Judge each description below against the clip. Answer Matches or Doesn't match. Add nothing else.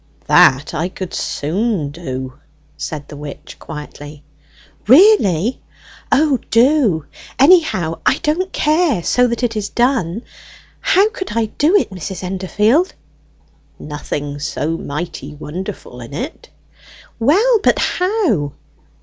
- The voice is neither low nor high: Doesn't match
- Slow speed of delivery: Matches